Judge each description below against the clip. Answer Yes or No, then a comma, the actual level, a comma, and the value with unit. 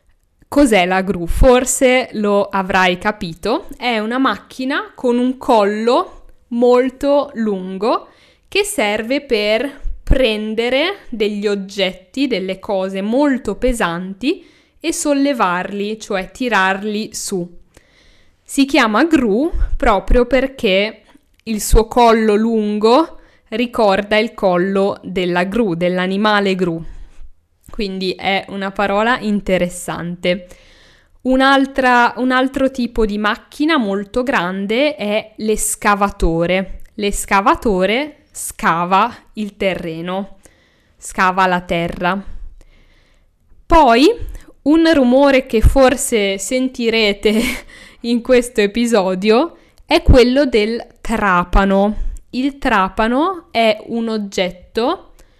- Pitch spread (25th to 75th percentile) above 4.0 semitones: Yes, average, 4.9 semitones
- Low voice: No, high, 220 Hz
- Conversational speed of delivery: No, slow, 95 wpm